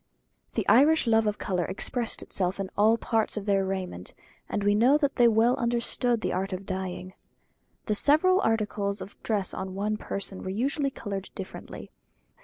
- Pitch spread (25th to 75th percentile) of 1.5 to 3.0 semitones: No, average, 3.6 semitones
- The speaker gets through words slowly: No, average, 175 wpm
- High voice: Yes, high, 210 Hz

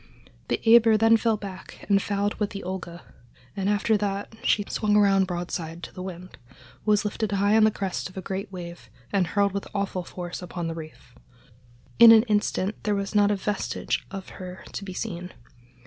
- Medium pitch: No, high, 200 Hz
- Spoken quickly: No, average, 195 wpm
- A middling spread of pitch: No, narrow, 2.3 semitones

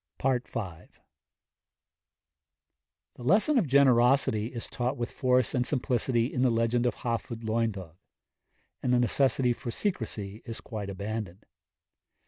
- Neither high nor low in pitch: No, low, 120 Hz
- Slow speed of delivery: Yes, slow, 120 wpm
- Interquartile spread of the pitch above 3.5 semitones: No, narrow, 2.5 semitones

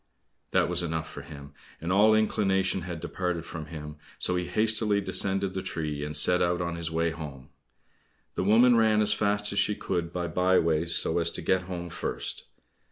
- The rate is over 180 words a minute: Yes, average, 195 wpm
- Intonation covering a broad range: No, average, 3.4 semitones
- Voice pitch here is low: Yes, very low, 90 Hz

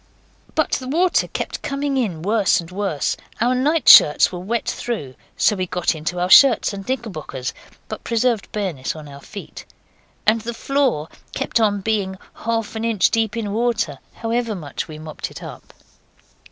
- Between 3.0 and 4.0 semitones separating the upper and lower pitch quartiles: No, average, 4.8 semitones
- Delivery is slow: No, average, 170 wpm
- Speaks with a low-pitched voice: No, high, 215 Hz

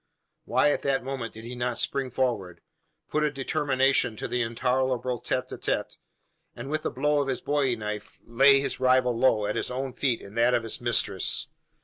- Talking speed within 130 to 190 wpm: No, average, 200 wpm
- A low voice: Yes, low, 125 Hz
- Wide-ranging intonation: No, average, 2.7 semitones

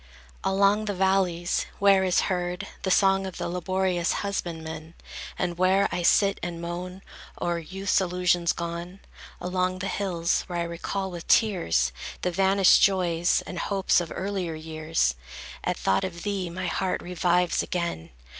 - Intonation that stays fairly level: Yes, narrow, 2.0 semitones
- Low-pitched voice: No, medium, 180 Hz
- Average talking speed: Yes, average, 150 wpm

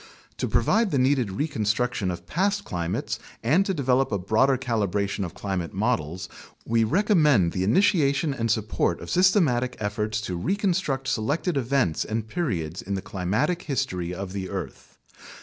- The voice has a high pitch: No, low, 115 Hz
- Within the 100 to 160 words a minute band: Yes, average, 150 wpm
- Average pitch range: No, wide, 6.9 semitones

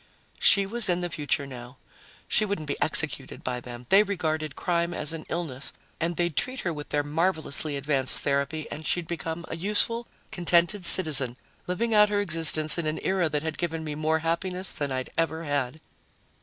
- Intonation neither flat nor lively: Yes, average, 3.3 semitones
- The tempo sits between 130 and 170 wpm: No, average, 185 wpm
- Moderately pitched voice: Yes, medium, 160 Hz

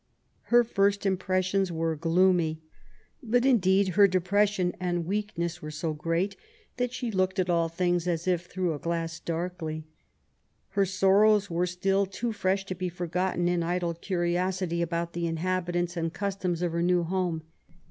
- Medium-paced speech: Yes, average, 160 wpm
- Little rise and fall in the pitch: Yes, narrow, 2.2 semitones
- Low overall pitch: No, medium, 180 Hz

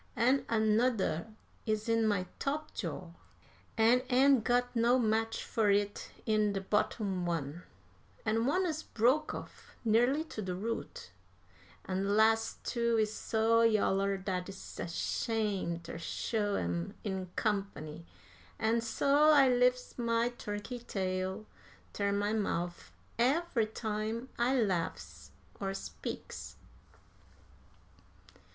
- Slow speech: Yes, slow, 120 wpm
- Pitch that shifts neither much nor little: Yes, average, 3.5 semitones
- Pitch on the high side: Yes, high, 220 Hz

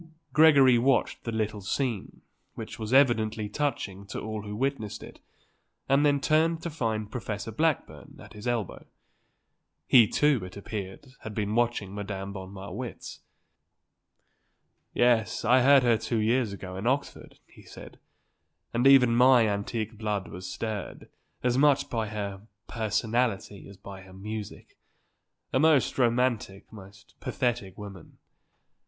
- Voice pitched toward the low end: Yes, low, 110 Hz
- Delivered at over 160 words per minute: No, average, 140 wpm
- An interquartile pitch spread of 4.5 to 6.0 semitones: No, average, 4.0 semitones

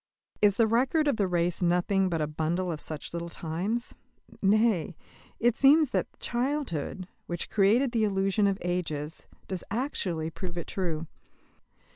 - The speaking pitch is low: No, high, 190 Hz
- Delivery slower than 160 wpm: Yes, average, 150 wpm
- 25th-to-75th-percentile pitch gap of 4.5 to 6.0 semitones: Yes, average, 5.1 semitones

